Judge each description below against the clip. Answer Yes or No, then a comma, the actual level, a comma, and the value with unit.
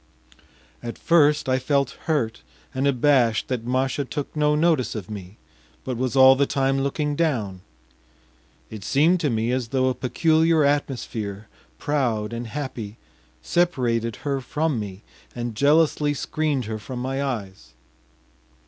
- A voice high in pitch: No, low, 130 Hz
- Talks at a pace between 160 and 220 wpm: No, average, 140 wpm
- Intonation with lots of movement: No, average, 4.1 semitones